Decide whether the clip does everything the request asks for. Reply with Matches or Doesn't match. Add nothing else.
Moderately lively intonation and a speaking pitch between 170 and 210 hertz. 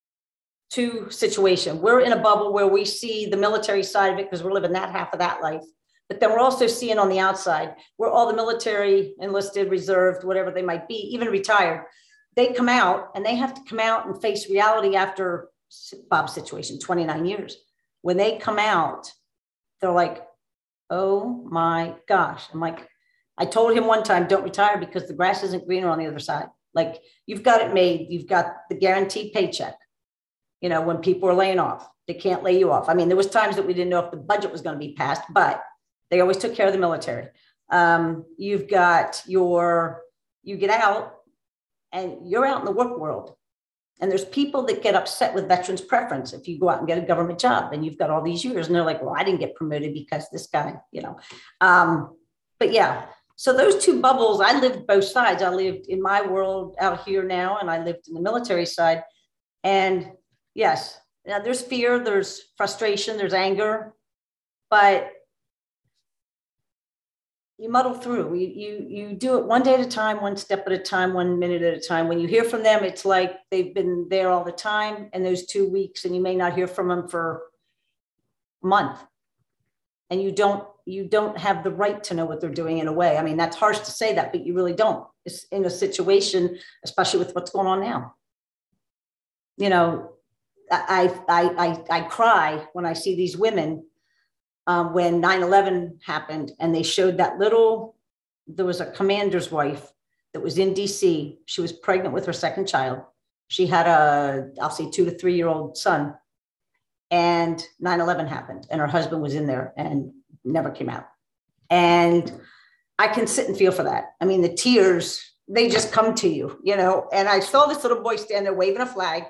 Matches